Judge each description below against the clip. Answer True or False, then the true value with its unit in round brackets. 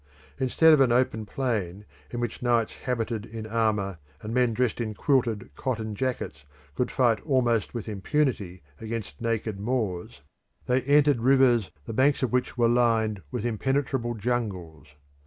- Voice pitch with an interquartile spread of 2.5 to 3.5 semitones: True (3.0 semitones)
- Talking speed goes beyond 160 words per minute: False (150 wpm)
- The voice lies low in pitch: True (115 Hz)